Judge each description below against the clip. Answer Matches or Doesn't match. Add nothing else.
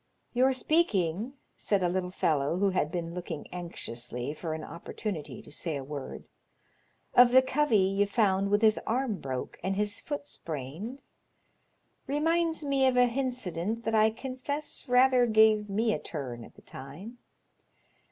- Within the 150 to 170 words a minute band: Matches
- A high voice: Matches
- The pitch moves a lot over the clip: Matches